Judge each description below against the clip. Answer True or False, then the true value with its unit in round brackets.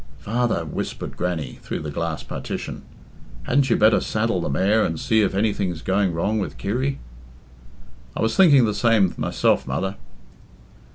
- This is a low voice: True (100 Hz)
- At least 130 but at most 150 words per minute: False (160 wpm)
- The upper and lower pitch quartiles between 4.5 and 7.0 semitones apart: True (5.0 semitones)